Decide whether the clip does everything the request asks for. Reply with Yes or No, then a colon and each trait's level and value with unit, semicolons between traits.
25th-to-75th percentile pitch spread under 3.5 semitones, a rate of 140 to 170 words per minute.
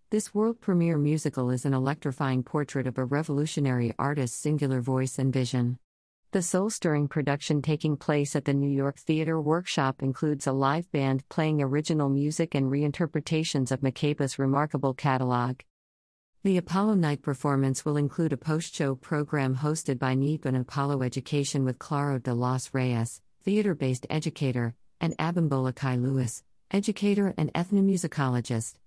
Yes: average, 2.9 semitones; average, 150 wpm